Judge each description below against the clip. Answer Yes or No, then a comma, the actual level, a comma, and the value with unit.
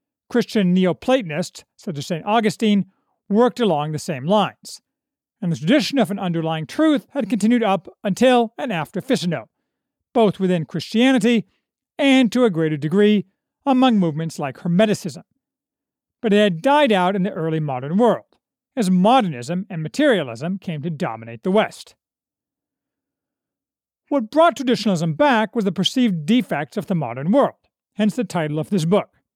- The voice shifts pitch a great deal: Yes, wide, 5.9 semitones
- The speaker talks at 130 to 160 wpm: Yes, average, 150 wpm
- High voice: Yes, high, 205 Hz